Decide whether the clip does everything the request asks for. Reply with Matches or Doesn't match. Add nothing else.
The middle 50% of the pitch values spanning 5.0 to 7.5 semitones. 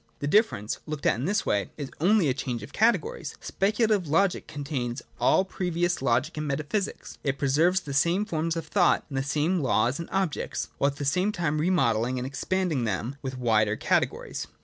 Matches